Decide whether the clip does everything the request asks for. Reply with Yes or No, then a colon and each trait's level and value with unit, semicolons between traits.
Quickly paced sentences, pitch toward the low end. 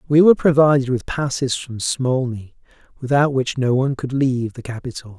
No: average, 175 wpm; low, 130 Hz